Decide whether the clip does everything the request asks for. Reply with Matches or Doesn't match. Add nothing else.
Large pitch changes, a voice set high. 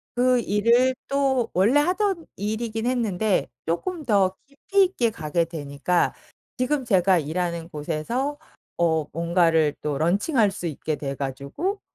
Matches